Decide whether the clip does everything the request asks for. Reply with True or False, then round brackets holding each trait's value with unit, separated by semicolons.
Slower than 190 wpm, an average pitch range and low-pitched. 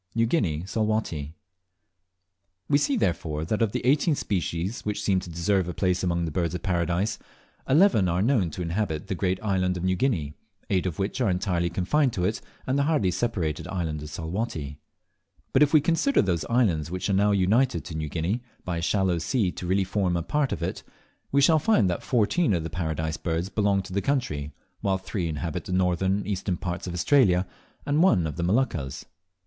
False (200 wpm; 4.5 semitones; 95 Hz)